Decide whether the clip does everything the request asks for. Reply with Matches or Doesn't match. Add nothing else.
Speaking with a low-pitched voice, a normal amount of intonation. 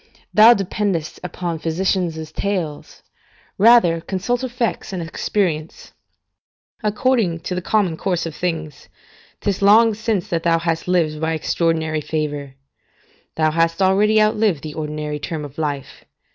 Doesn't match